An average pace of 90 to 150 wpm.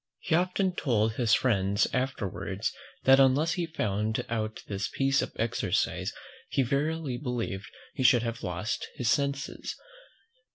Yes: average, 140 wpm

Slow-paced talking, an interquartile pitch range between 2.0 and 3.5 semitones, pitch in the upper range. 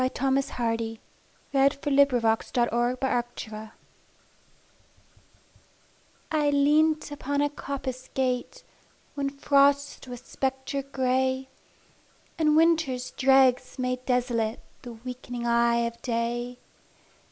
Yes: slow, 90 wpm; average, 2.7 semitones; very high, 260 Hz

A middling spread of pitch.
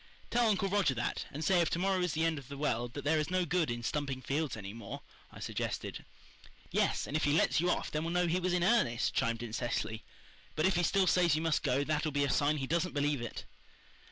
Yes: average, 4.8 semitones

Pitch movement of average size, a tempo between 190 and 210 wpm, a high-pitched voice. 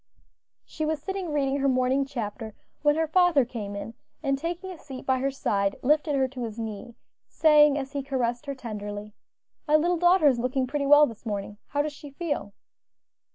Yes: average, 4.0 semitones; average, 195 wpm; very high, 275 Hz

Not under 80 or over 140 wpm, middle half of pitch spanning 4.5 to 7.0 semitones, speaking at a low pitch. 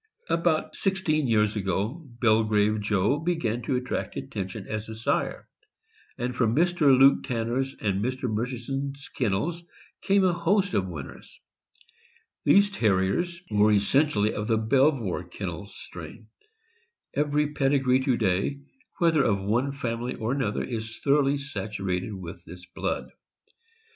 Yes: slow, 135 wpm; average, 5.2 semitones; low, 120 Hz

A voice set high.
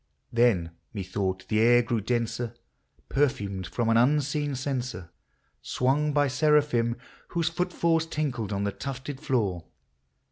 No: low, 125 Hz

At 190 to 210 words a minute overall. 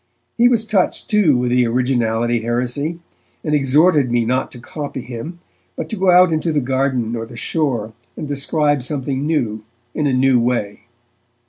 No: average, 170 wpm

